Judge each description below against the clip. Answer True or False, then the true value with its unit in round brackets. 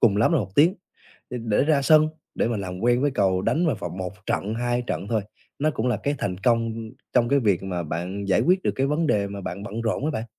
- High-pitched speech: False (115 Hz)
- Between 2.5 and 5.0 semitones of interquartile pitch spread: False (5.5 semitones)